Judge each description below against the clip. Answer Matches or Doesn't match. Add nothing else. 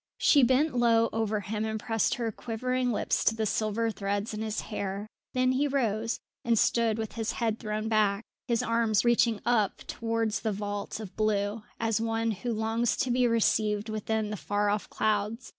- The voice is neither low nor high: Doesn't match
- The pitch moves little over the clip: Matches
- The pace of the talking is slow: Doesn't match